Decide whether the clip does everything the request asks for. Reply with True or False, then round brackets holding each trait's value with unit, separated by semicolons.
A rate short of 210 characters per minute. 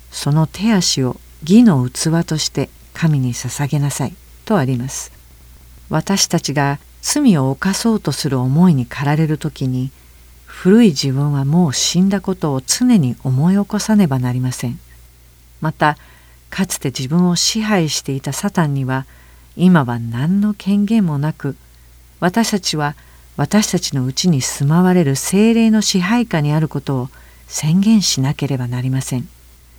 False (285 characters per minute)